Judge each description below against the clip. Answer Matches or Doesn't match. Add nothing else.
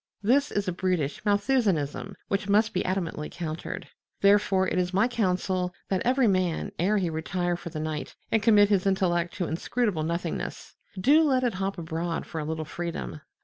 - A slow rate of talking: Doesn't match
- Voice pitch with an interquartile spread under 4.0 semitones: Matches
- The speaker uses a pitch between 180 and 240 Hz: Matches